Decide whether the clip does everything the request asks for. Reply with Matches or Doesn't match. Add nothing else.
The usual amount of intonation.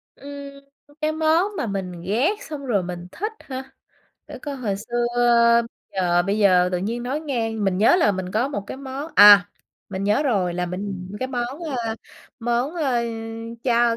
Doesn't match